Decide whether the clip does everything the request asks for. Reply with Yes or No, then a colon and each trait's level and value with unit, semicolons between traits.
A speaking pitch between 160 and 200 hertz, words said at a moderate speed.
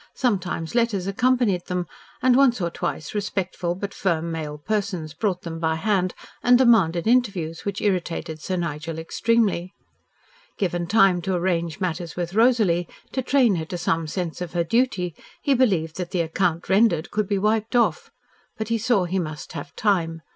Yes: medium, 185 Hz; average, 170 wpm